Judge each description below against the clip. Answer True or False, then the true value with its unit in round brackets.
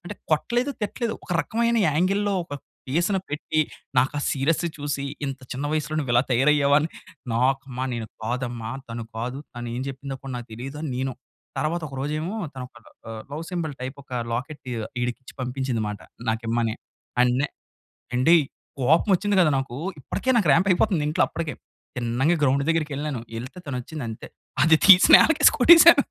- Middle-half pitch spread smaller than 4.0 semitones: False (4.8 semitones)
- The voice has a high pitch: False (140 Hz)